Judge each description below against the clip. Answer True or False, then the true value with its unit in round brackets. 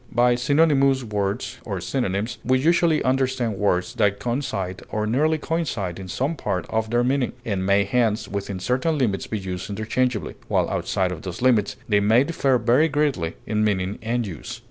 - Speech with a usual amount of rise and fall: True (4.9 semitones)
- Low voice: True (115 Hz)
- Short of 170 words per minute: False (175 wpm)